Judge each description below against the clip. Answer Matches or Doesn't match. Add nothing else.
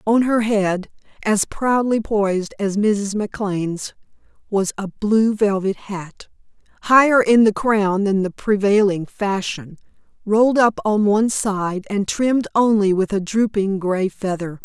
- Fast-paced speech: Doesn't match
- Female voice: Matches